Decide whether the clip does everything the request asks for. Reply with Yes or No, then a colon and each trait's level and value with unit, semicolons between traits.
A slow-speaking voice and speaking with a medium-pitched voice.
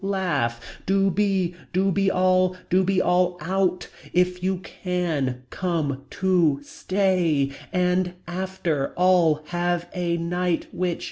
Yes: slow, 125 wpm; medium, 180 Hz